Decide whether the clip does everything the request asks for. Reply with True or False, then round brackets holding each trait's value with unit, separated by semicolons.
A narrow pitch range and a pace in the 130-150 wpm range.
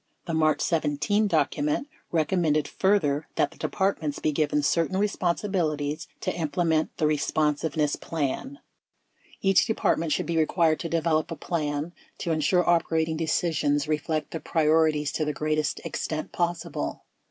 True (2.2 semitones; 140 wpm)